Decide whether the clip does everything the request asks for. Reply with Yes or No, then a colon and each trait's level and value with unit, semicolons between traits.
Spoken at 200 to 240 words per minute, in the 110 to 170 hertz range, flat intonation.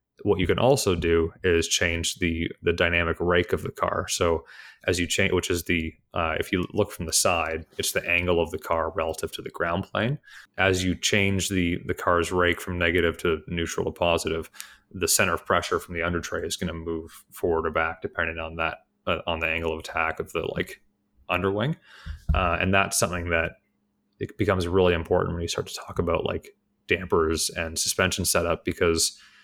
No: fast, 205 wpm; very low, 85 Hz; narrow, 2.0 semitones